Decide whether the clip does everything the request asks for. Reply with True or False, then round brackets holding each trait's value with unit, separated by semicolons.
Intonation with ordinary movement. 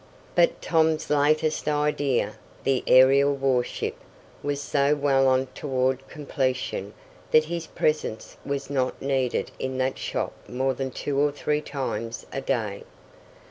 False (2.1 semitones)